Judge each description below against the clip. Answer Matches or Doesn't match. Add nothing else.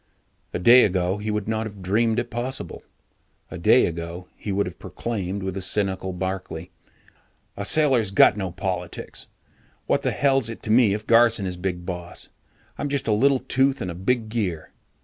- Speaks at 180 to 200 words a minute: Matches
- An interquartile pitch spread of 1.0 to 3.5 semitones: Doesn't match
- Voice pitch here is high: Doesn't match